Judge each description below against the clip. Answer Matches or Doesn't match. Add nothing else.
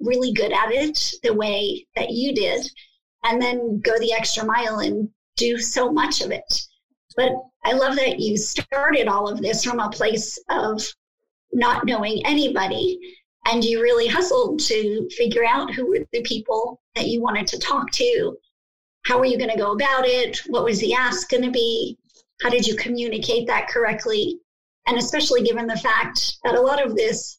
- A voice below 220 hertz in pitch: Doesn't match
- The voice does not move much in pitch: Doesn't match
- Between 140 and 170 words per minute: Doesn't match